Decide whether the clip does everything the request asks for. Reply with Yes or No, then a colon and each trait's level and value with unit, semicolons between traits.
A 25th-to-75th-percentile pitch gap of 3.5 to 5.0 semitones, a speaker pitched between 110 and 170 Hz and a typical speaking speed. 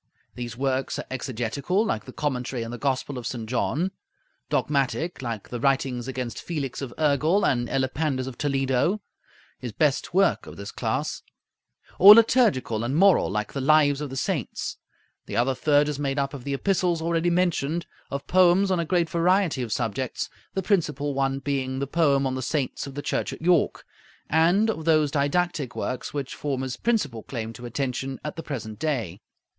Yes: average, 4.2 semitones; medium, 140 Hz; average, 185 wpm